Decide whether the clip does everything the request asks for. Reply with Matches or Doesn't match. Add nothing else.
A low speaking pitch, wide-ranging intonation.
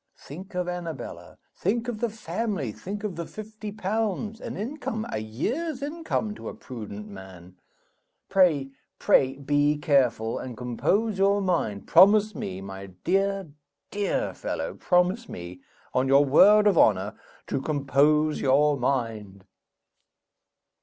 Doesn't match